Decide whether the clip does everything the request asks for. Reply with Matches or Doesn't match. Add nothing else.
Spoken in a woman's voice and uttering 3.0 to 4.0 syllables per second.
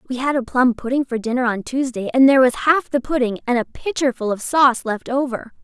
Doesn't match